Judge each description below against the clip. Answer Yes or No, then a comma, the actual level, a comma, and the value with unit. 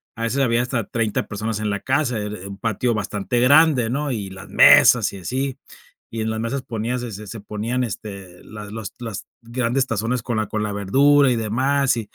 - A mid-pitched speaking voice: No, low, 115 Hz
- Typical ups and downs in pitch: Yes, average, 3.1 semitones